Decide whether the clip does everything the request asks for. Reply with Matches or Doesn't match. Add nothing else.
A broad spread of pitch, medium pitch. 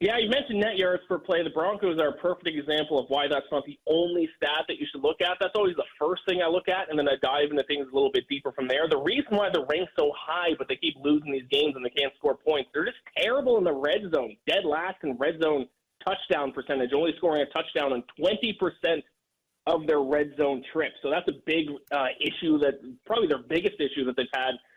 Matches